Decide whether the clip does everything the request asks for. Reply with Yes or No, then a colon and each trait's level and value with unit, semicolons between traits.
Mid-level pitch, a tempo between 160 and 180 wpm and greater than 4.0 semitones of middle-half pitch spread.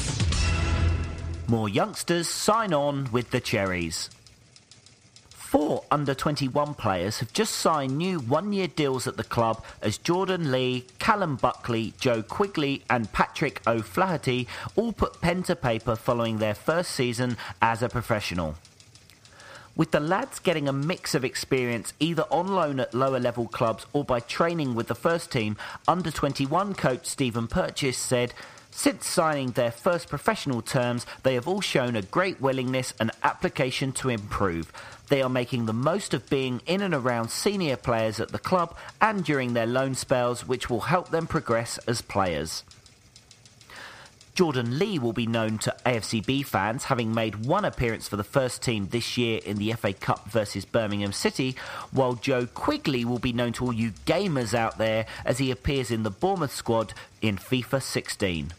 No: low, 125 Hz; average, 165 wpm; average, 4.4 semitones